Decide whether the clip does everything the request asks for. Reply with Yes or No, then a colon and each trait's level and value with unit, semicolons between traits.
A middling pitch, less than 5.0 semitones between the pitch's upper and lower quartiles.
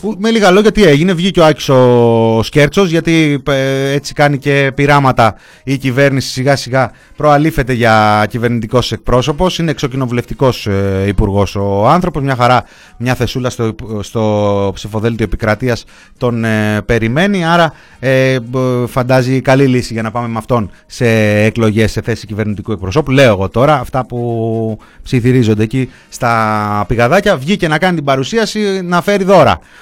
No: low, 125 Hz; average, 4.4 semitones